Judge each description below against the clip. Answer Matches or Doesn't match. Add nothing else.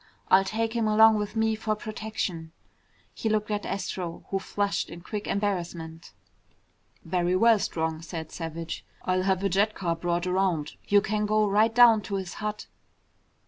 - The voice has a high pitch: Matches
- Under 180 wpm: Matches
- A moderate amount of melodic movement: Matches